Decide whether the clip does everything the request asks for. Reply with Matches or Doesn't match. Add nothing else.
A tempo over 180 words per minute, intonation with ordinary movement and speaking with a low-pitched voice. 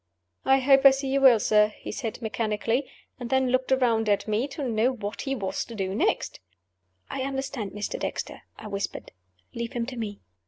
Doesn't match